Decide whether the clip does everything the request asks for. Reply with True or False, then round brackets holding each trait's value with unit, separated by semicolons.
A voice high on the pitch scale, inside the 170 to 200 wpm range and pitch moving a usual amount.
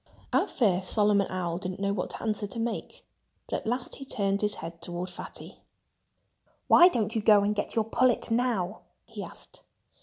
True (205 Hz; 180 wpm; 3.4 semitones)